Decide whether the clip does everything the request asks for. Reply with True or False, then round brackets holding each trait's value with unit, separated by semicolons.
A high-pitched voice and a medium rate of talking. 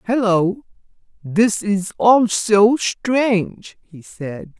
False (205 Hz; 90 wpm)